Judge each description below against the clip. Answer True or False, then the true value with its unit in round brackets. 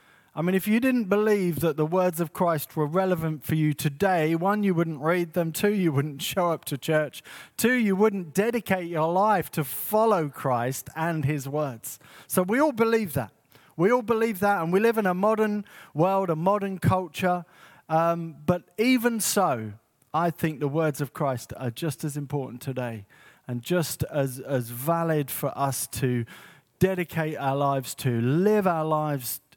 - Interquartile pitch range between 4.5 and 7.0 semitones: True (5.1 semitones)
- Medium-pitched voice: True (165 Hz)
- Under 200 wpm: True (180 wpm)